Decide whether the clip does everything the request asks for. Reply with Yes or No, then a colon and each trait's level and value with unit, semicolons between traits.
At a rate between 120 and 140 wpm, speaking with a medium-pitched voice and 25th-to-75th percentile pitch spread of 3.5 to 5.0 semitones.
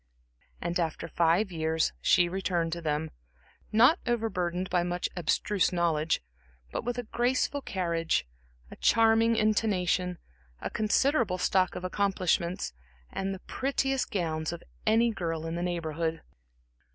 Yes: slow, 135 wpm; medium, 180 Hz; average, 4.5 semitones